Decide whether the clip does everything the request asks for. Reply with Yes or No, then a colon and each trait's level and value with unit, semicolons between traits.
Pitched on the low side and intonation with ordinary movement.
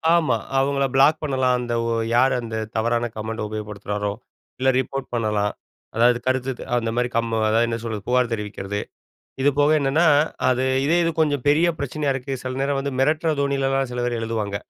Yes: low, 125 Hz; average, 3.3 semitones